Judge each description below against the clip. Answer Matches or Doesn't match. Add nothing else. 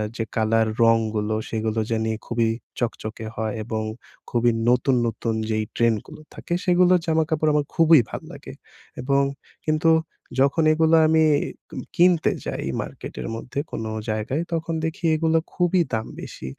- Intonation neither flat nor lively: Doesn't match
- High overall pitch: Doesn't match